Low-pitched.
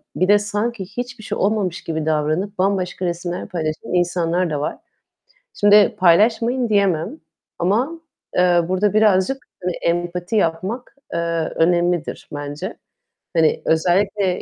No: medium, 185 Hz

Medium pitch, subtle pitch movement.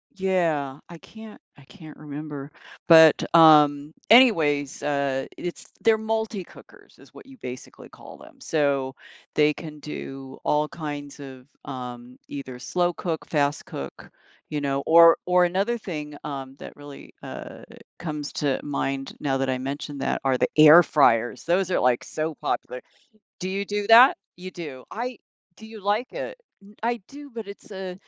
No: medium, 150 Hz; average, 5.2 semitones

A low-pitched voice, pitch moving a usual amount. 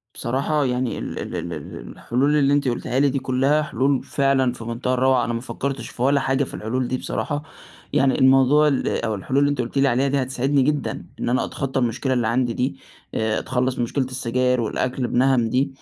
No: low, 130 Hz; narrow, 1.9 semitones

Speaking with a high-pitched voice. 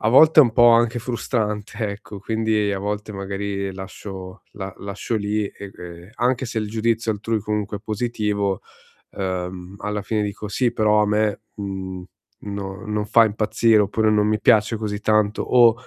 No: low, 105 Hz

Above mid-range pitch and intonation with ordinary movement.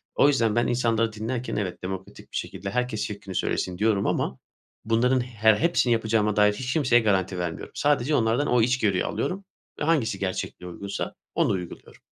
No: low, 110 Hz; average, 4.0 semitones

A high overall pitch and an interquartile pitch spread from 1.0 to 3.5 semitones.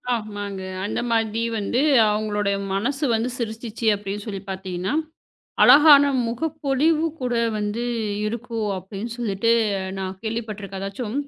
Yes: high, 215 Hz; average, 3.2 semitones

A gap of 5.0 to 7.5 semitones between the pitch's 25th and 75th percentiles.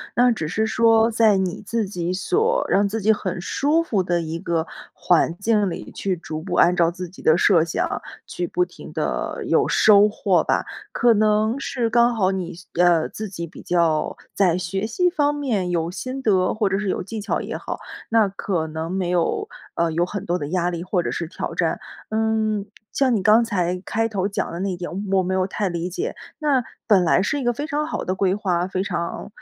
No: average, 4.0 semitones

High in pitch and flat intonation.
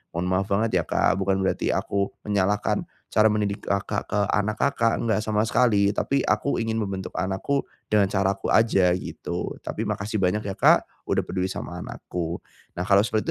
No: low, 100 Hz; narrow, 2.1 semitones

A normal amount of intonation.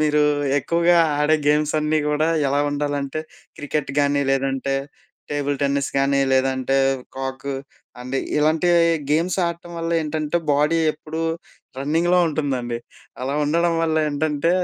No: narrow, 2.3 semitones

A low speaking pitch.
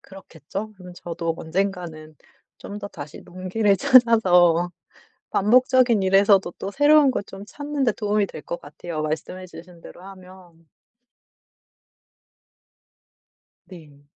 No: high, 190 Hz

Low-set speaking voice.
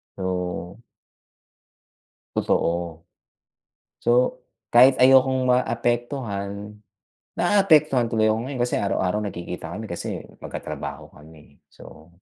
Yes: low, 110 Hz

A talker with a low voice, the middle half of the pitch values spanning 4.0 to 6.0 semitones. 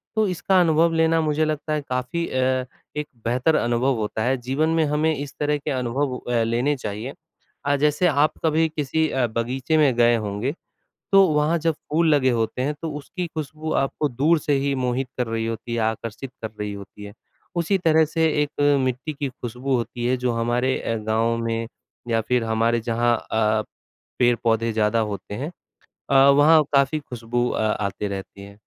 Yes: low, 130 Hz; average, 4.8 semitones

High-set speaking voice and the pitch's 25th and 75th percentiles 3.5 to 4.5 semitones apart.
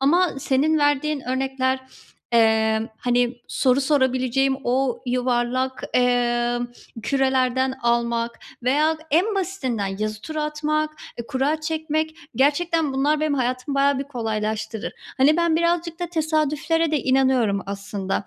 Yes: very high, 265 Hz; average, 4.1 semitones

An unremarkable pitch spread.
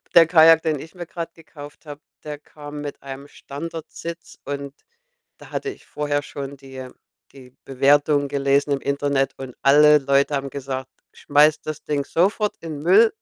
No: narrow, 2.3 semitones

